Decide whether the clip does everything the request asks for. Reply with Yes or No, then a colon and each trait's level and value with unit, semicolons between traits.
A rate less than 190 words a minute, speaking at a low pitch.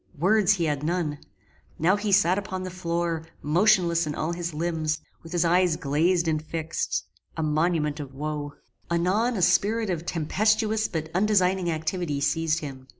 No: average, 160 wpm; medium, 170 Hz